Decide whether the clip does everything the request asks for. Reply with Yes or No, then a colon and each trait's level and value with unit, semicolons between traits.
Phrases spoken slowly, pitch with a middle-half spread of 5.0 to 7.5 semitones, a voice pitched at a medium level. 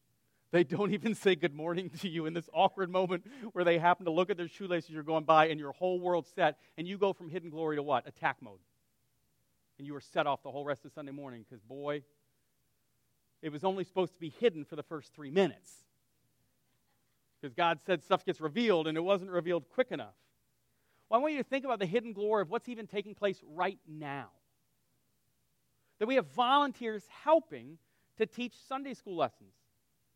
No: fast, 205 wpm; average, 5.3 semitones; medium, 175 Hz